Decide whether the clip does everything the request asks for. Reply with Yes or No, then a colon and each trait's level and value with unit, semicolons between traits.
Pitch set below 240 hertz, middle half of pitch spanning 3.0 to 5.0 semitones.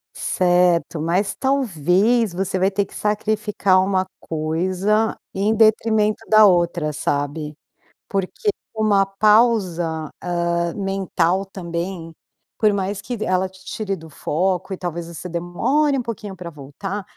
Yes: high, 190 Hz; average, 3.5 semitones